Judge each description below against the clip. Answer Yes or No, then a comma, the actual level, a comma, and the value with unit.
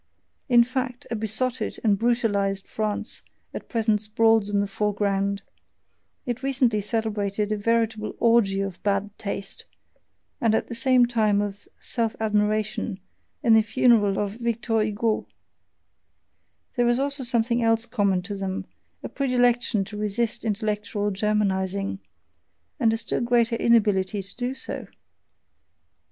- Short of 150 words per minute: Yes, slow, 135 wpm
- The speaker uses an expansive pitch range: No, narrow, 2.6 semitones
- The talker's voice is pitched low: No, high, 220 Hz